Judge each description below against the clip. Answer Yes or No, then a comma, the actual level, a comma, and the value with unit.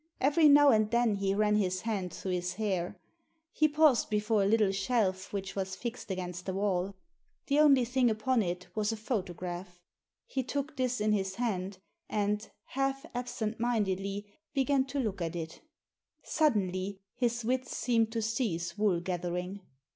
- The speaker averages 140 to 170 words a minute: Yes, average, 160 wpm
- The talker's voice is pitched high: Yes, high, 210 Hz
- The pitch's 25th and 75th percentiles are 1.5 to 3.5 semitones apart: No, average, 4.5 semitones